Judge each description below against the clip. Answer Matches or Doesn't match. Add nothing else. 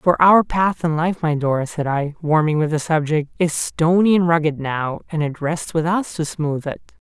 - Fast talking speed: Matches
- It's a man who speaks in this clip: Matches